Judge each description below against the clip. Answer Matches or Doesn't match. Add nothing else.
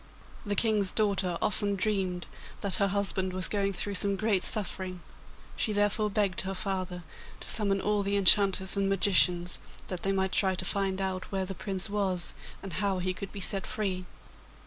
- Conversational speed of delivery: Matches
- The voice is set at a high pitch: Matches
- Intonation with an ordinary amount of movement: Doesn't match